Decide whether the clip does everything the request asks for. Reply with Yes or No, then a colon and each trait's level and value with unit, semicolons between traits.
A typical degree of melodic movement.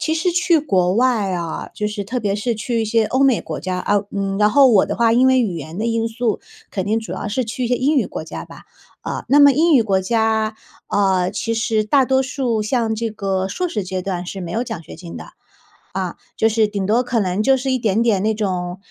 Yes: average, 4.1 semitones